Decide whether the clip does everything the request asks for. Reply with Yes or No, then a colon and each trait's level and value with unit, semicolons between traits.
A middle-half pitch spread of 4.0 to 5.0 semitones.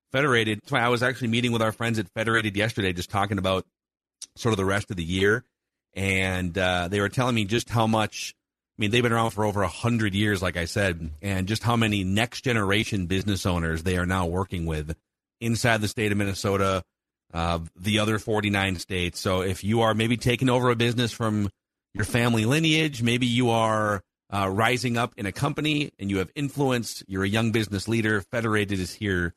No: average, 3.4 semitones